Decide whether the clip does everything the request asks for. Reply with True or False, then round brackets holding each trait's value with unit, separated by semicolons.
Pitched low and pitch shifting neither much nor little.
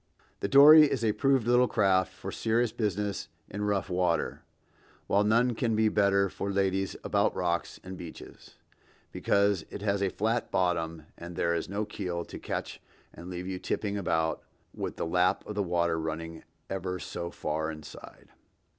True (95 Hz; 3.4 semitones)